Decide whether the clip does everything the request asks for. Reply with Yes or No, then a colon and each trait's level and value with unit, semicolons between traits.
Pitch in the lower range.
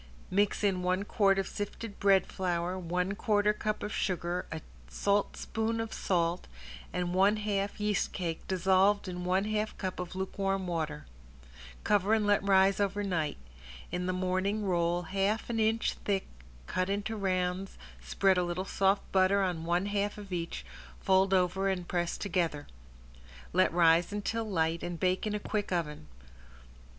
No: high, 190 Hz